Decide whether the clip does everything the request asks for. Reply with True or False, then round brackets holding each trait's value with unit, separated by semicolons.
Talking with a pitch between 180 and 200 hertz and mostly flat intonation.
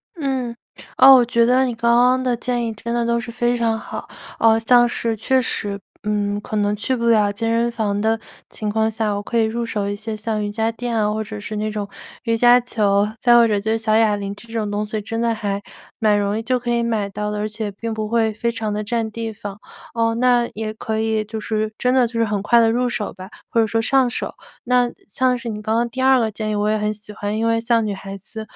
False (225 Hz; 2.0 semitones)